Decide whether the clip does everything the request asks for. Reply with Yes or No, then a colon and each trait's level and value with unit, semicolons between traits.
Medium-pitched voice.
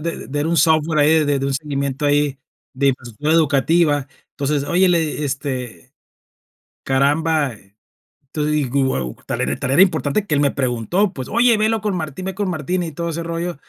Yes: medium, 150 Hz